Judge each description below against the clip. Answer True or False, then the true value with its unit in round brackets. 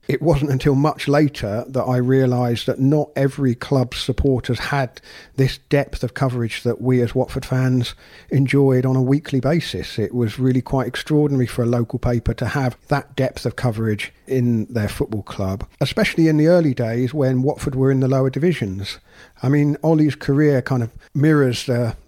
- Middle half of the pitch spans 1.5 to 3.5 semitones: True (2.6 semitones)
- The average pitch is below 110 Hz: False (130 Hz)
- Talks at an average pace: True (180 wpm)